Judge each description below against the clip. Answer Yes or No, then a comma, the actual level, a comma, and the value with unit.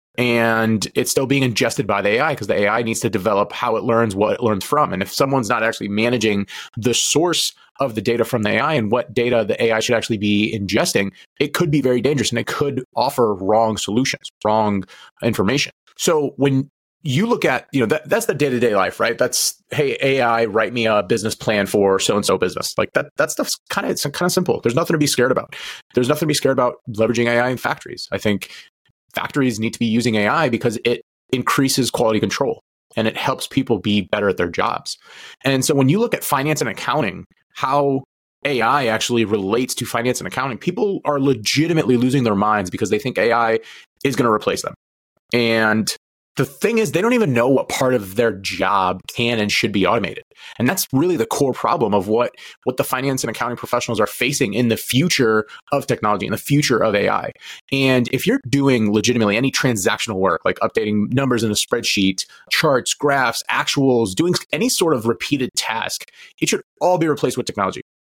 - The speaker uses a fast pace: Yes, fast, 210 wpm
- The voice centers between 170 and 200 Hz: No, low, 120 Hz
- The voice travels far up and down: No, average, 3.7 semitones